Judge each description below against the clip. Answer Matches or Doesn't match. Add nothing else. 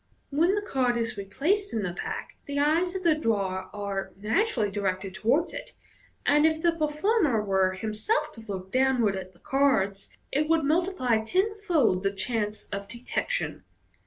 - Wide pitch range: Matches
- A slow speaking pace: Doesn't match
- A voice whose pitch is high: Matches